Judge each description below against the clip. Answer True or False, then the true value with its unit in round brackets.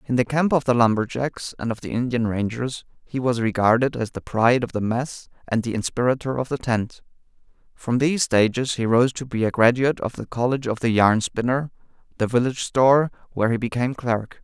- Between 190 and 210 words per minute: True (205 wpm)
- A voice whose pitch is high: False (120 Hz)